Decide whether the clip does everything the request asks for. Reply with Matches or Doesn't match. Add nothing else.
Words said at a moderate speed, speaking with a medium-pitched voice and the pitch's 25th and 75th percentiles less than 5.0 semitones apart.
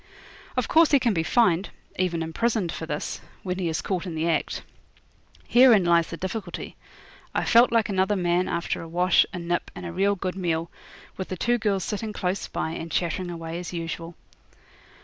Matches